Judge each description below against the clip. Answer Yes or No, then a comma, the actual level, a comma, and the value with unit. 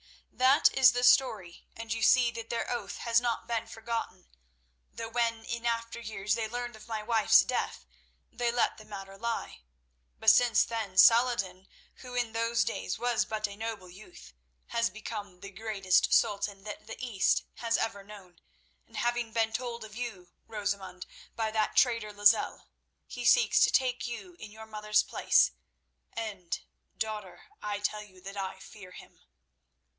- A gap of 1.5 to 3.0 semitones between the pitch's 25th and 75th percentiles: Yes, narrow, 2.5 semitones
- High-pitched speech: Yes, high, 220 Hz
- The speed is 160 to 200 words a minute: Yes, average, 165 wpm